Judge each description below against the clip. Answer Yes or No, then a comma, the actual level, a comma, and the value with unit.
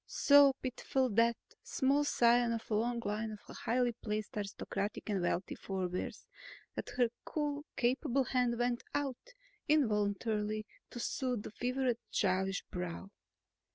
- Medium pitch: No, high, 235 Hz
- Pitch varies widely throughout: No, average, 3.6 semitones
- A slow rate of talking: Yes, slow, 130 wpm